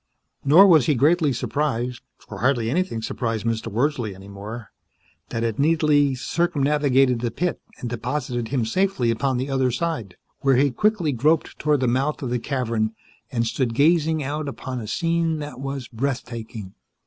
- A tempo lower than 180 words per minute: Yes, average, 165 wpm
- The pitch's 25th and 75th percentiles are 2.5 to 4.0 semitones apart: No, average, 4.4 semitones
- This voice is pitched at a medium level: No, low, 130 Hz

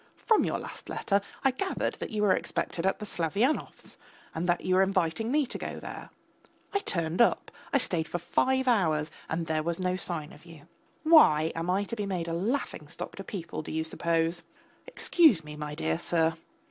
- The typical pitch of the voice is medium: Yes, medium, 175 Hz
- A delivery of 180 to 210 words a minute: Yes, average, 200 wpm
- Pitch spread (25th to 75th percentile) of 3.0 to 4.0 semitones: No, average, 5.1 semitones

